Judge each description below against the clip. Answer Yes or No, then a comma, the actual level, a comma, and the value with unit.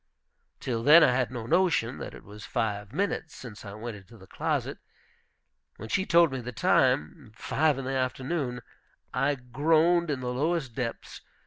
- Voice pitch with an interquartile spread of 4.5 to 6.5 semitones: Yes, average, 5.1 semitones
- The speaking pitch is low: Yes, low, 130 Hz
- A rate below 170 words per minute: No, average, 175 wpm